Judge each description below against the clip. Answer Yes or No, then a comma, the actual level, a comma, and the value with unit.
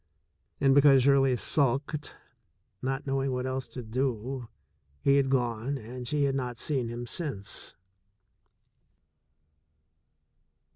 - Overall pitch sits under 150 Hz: Yes, low, 135 Hz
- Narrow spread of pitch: Yes, narrow, 2.1 semitones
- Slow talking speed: Yes, slow, 110 wpm